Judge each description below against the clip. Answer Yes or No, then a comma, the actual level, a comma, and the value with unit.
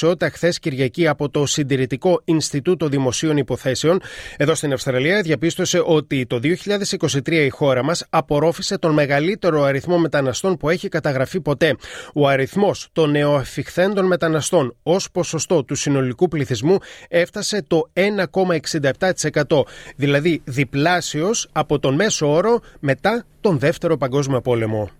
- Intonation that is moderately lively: Yes, average, 3.8 semitones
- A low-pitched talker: No, medium, 155 Hz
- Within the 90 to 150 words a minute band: Yes, average, 125 wpm